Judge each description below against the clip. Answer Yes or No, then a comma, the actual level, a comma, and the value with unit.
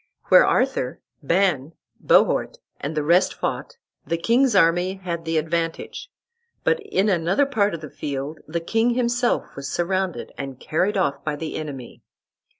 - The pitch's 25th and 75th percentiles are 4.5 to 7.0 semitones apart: Yes, average, 5.0 semitones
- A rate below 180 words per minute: Yes, average, 150 wpm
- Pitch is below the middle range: No, medium, 170 Hz